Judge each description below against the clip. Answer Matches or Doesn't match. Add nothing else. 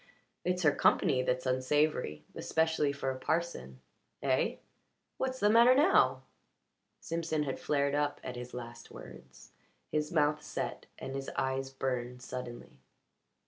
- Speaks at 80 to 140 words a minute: Matches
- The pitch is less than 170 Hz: Matches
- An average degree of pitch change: Matches